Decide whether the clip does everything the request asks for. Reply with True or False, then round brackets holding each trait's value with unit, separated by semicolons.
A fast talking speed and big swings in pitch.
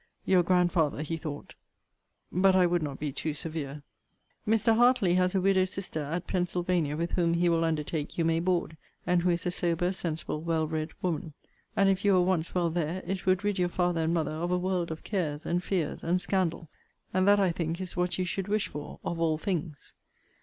False (210 wpm; 2.4 semitones)